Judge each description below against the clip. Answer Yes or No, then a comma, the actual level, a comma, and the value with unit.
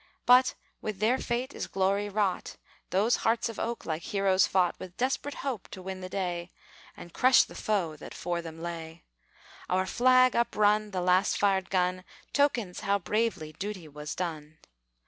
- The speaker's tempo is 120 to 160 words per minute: No, average, 170 wpm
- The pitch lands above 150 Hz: Yes, high, 190 Hz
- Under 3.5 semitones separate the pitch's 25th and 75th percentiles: No, average, 4.2 semitones